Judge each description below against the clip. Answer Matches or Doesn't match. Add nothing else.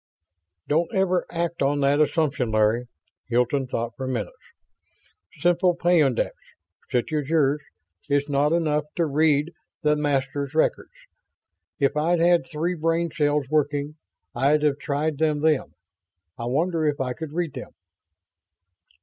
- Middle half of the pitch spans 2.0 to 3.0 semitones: Matches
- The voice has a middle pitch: Matches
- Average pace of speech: Doesn't match